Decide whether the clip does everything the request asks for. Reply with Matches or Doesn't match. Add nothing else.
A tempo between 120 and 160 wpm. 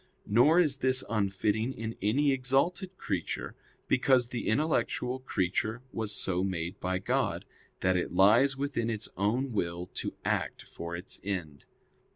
Matches